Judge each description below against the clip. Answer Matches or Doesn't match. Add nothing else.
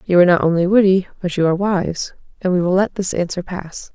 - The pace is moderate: Doesn't match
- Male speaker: Doesn't match